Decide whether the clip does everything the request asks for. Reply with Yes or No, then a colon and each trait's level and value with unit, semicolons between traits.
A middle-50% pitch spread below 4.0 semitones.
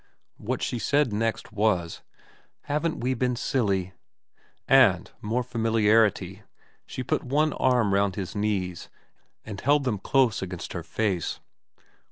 No: average, 4.4 semitones